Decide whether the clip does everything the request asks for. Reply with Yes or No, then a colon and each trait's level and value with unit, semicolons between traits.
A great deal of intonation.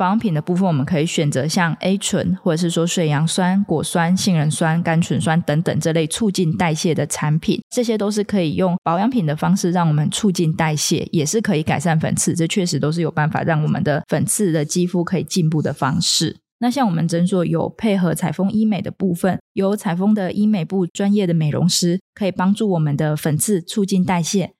No: average, 3.0 semitones